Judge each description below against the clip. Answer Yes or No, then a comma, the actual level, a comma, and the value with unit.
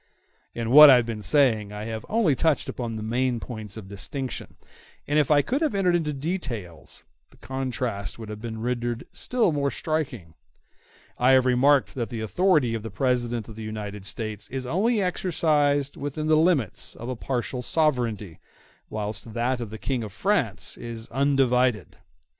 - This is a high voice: No, low, 125 Hz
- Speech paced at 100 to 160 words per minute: No, average, 175 wpm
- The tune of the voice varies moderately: Yes, average, 4.7 semitones